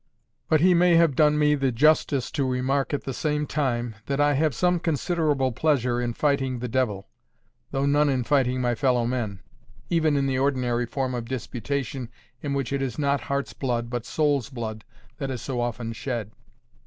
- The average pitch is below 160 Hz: Yes, low, 135 Hz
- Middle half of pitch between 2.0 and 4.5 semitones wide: Yes, average, 3.2 semitones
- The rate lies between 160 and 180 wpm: No, average, 190 wpm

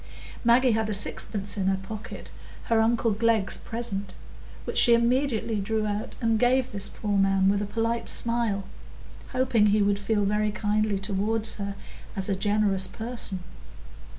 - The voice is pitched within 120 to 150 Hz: No, high, 215 Hz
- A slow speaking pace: No, average, 150 wpm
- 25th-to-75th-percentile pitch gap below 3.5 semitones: Yes, narrow, 2.4 semitones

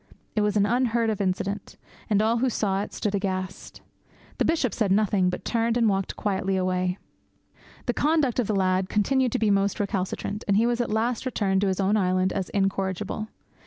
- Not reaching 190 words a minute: No, average, 200 wpm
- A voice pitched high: Yes, high, 205 Hz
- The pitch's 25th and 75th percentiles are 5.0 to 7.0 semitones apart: No, average, 3.0 semitones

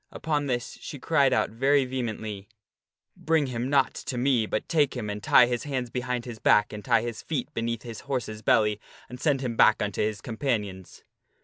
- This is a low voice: Yes, low, 120 Hz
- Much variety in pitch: No, average, 3.5 semitones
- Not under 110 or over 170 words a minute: No, average, 200 wpm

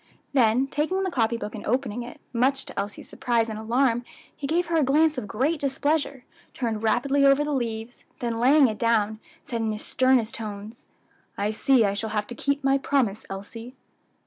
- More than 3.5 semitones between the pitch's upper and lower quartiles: Yes, average, 3.9 semitones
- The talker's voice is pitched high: Yes, high, 245 Hz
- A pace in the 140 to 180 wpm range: No, average, 195 wpm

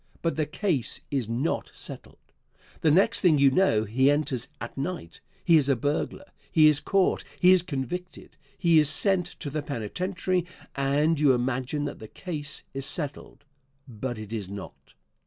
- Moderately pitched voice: Yes, medium, 145 Hz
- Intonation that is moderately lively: Yes, average, 4.8 semitones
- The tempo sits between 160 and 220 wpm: Yes, average, 170 wpm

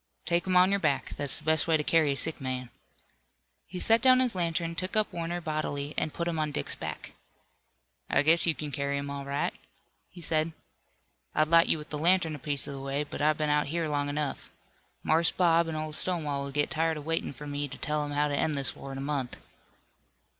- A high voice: No, medium, 155 Hz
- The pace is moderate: No, fast, 230 wpm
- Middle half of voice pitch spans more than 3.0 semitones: No, narrow, 2.6 semitones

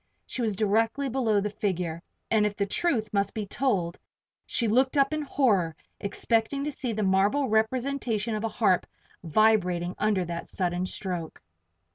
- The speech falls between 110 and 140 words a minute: No, average, 160 wpm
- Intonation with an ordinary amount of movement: Yes, average, 4.3 semitones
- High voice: Yes, high, 215 Hz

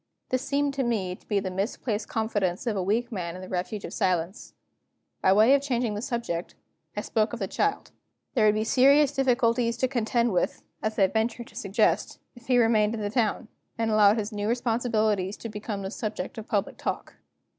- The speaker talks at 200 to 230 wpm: Yes, fast, 205 wpm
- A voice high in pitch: Yes, high, 220 Hz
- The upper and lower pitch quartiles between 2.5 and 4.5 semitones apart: Yes, average, 2.9 semitones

